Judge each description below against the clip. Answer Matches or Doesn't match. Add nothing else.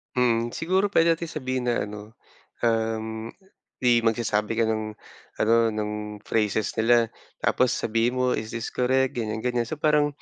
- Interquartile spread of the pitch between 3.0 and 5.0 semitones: Doesn't match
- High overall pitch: Doesn't match